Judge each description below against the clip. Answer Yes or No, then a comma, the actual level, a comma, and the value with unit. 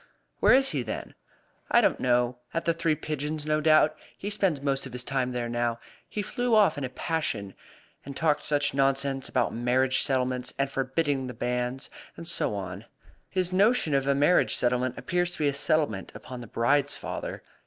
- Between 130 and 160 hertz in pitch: Yes, medium, 140 Hz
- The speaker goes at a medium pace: Yes, average, 190 wpm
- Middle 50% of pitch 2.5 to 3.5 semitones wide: No, average, 4.0 semitones